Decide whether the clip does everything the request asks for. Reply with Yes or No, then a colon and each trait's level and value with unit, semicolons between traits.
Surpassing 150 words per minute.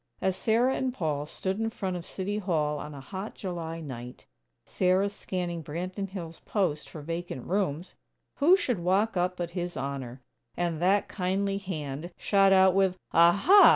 Yes: average, 165 wpm